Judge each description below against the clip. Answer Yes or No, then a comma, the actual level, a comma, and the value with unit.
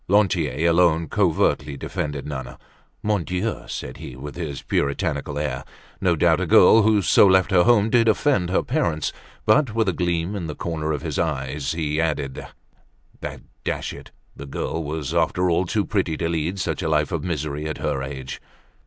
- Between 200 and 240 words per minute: No, average, 185 wpm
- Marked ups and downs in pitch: No, average, 4.3 semitones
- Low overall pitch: Yes, very low, 80 Hz